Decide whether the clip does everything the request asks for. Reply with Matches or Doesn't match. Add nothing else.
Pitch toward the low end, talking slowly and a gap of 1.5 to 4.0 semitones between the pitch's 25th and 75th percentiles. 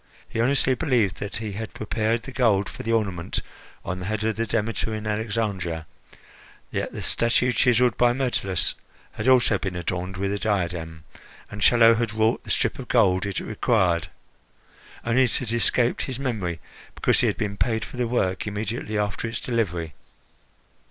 Doesn't match